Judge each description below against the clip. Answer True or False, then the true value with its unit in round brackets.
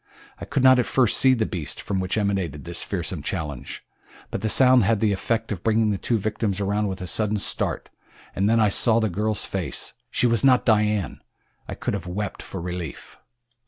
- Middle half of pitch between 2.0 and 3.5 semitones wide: True (3.2 semitones)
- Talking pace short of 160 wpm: False (205 wpm)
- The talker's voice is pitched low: True (105 Hz)